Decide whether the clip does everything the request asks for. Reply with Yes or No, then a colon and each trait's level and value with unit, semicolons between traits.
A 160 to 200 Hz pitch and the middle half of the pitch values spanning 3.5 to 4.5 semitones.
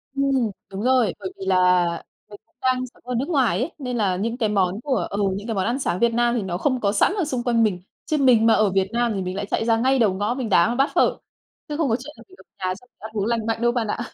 No: high, 230 Hz; average, 4.1 semitones